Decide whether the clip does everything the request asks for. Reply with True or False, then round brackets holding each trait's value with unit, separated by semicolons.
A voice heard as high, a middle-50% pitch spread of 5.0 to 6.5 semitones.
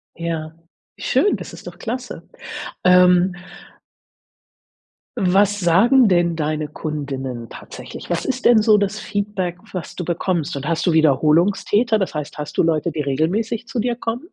False (180 Hz; 5.3 semitones)